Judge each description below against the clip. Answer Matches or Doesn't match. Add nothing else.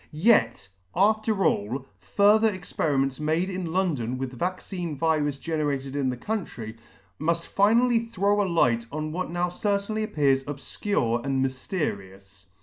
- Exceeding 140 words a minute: Doesn't match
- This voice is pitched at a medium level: Matches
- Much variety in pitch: Matches